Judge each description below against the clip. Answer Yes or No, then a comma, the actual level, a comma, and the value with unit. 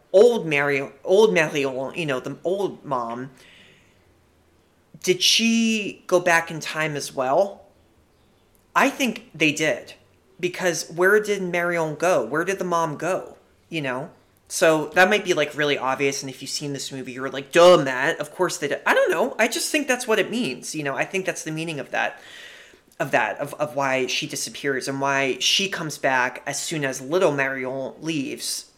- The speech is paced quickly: No, average, 190 wpm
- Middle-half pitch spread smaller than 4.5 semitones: No, average, 4.9 semitones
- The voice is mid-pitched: Yes, medium, 155 Hz